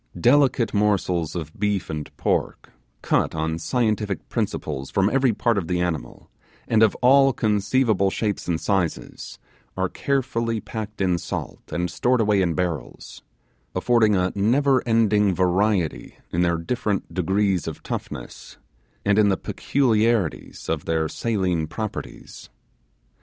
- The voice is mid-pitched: No, low, 100 Hz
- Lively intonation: No, average, 4.4 semitones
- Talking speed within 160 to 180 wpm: No, slow, 135 wpm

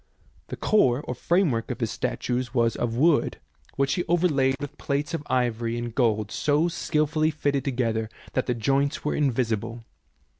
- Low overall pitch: Yes, low, 130 Hz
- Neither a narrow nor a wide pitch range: Yes, average, 4.0 semitones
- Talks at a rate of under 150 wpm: No, average, 165 wpm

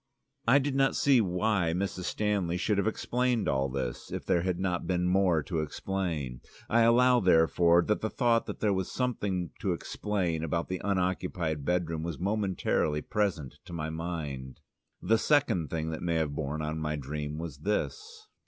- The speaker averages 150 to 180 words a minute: Yes, average, 175 wpm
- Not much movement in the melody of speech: No, average, 4.9 semitones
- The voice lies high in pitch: No, very low, 90 Hz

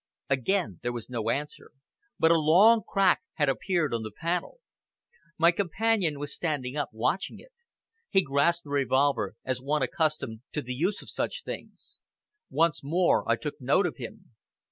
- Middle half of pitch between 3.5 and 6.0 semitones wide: Yes, average, 5.2 semitones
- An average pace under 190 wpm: Yes, average, 165 wpm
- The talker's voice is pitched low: No, medium, 150 Hz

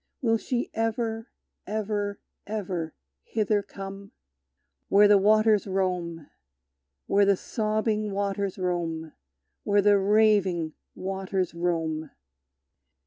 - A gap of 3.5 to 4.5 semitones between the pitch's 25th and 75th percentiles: No, average, 2.7 semitones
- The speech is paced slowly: Yes, slow, 95 wpm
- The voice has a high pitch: Yes, high, 200 Hz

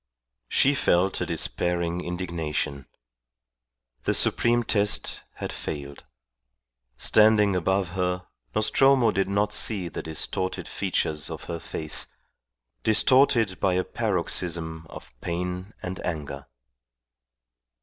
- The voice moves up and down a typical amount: Yes, average, 3.8 semitones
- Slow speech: Yes, slow, 105 wpm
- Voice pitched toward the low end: Yes, very low, 90 Hz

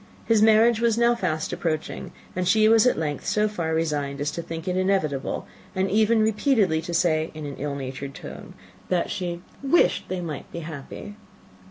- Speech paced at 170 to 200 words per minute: Yes, average, 185 wpm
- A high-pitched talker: No, medium, 175 Hz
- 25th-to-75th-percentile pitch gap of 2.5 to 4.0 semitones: No, wide, 5.6 semitones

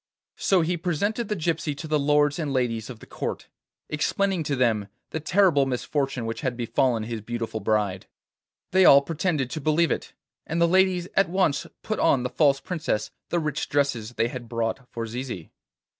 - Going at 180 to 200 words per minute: Yes, average, 185 wpm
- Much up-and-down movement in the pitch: Yes, wide, 6.0 semitones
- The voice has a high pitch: No, medium, 140 Hz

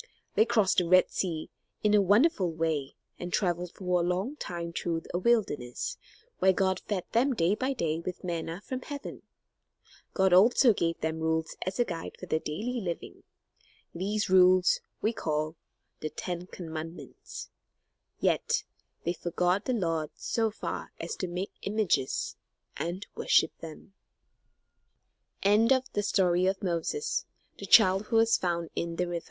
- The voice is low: No, medium, 180 Hz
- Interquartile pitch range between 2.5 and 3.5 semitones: No, average, 3.9 semitones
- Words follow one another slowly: Yes, slow, 125 wpm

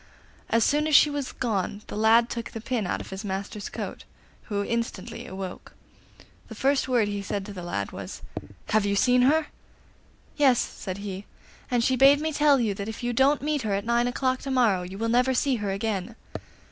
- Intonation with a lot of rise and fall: No, average, 4.5 semitones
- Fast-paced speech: Yes, fast, 210 wpm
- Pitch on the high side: Yes, high, 230 Hz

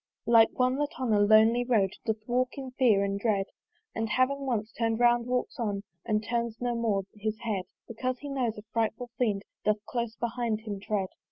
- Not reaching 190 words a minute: No, average, 195 wpm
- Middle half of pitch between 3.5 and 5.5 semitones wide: No, narrow, 2.5 semitones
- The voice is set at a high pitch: Yes, high, 230 Hz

